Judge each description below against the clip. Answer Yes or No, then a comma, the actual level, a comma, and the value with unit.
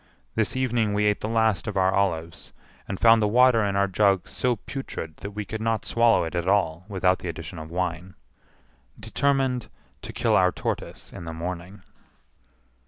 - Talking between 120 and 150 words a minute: No, average, 180 wpm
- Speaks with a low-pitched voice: Yes, low, 100 Hz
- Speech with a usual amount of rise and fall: Yes, average, 3.9 semitones